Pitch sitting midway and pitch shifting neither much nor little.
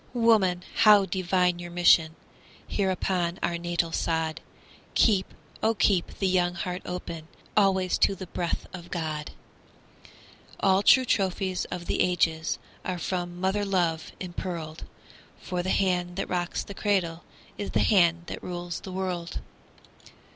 No: medium, 180 Hz; narrow, 1.7 semitones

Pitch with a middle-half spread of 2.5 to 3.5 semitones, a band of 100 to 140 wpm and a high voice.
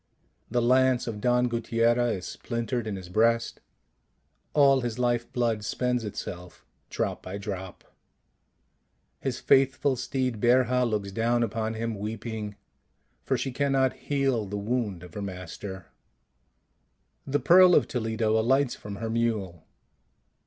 No: average, 3.2 semitones; slow, 135 wpm; low, 115 Hz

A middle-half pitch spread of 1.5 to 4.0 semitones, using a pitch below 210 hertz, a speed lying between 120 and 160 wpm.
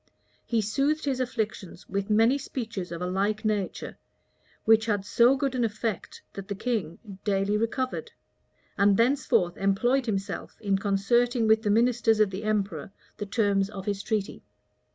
No: average, 3.2 semitones; high, 215 Hz; average, 155 wpm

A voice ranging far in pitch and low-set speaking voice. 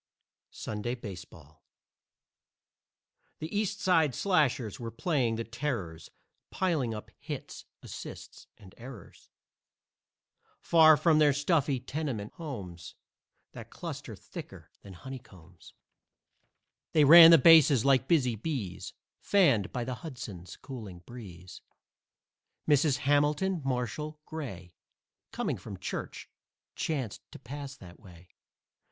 Yes: wide, 6.7 semitones; low, 130 Hz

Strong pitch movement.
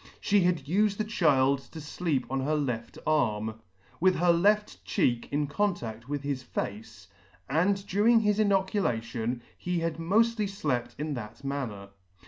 Yes: wide, 7.9 semitones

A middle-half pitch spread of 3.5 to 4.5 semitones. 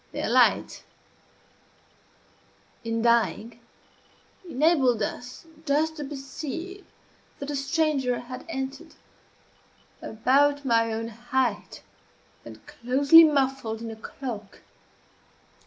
Yes: average, 3.8 semitones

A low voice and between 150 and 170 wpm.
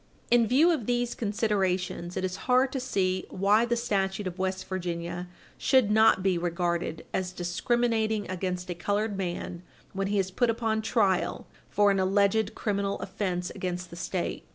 No: high, 195 Hz; average, 165 wpm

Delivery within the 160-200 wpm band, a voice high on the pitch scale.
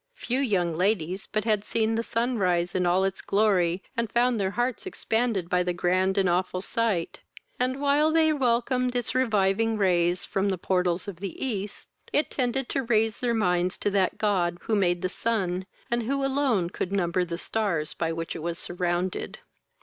Yes: average, 190 wpm; high, 200 Hz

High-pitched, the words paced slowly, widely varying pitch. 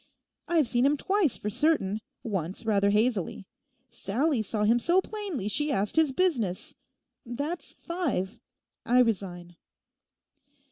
Yes: high, 240 Hz; slow, 125 wpm; wide, 7.4 semitones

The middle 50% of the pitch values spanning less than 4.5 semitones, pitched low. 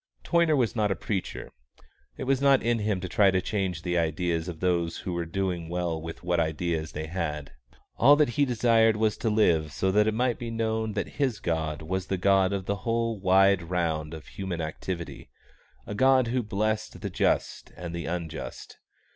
No: average, 4.8 semitones; very low, 95 Hz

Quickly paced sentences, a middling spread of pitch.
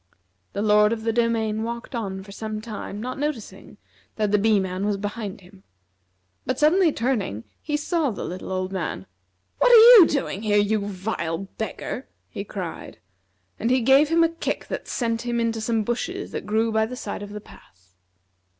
No: average, 185 wpm; average, 3.8 semitones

